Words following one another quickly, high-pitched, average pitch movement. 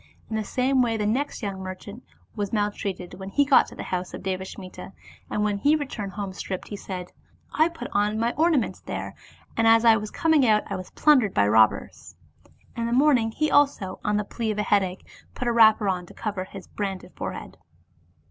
Yes: fast, 210 wpm; high, 210 Hz; average, 4.0 semitones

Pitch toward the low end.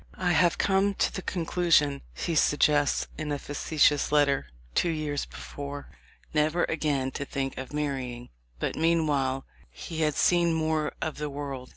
No: medium, 150 Hz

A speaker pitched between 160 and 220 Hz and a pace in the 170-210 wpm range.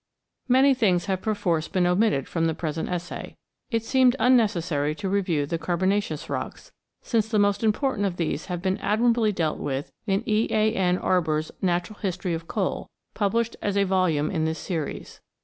Yes: medium, 185 Hz; average, 175 wpm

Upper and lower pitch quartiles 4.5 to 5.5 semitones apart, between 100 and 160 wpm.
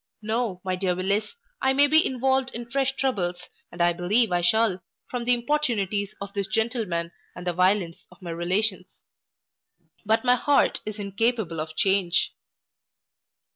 Yes: average, 5.0 semitones; average, 155 wpm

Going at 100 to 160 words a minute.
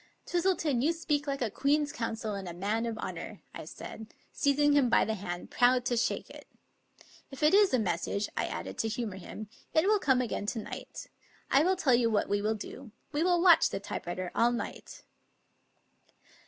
No: fast, 205 wpm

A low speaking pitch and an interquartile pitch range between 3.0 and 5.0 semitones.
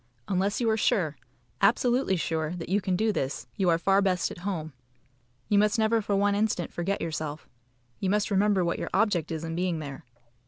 No: high, 190 Hz; average, 3.9 semitones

